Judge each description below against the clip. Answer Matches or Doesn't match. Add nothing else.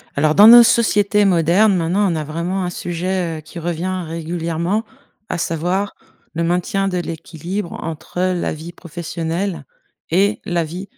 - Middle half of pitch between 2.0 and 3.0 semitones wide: Matches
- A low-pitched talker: Doesn't match